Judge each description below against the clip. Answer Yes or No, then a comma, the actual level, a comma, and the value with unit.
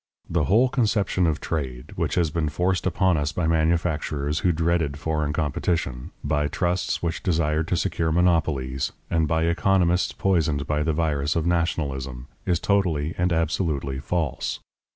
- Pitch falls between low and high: No, very low, 80 Hz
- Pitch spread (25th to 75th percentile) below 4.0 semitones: Yes, average, 2.9 semitones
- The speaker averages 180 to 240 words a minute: No, average, 150 wpm